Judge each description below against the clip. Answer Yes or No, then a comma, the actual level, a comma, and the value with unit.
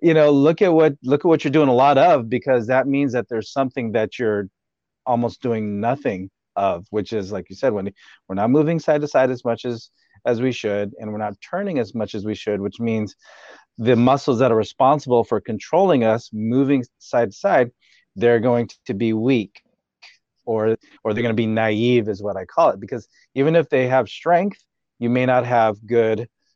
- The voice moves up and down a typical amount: Yes, average, 3.4 semitones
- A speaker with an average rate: No, fast, 210 wpm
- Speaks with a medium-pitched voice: No, low, 120 Hz